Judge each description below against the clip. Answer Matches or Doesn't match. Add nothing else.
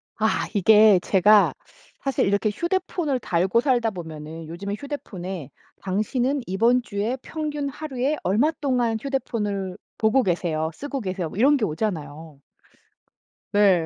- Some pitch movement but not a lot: Doesn't match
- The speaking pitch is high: Matches